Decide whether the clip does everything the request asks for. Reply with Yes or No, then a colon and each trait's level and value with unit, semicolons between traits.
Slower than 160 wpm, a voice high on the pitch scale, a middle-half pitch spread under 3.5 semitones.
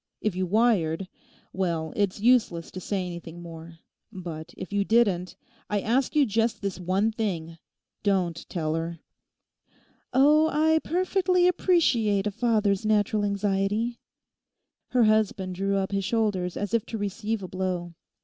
No: average, 145 wpm; high, 200 Hz; average, 3.9 semitones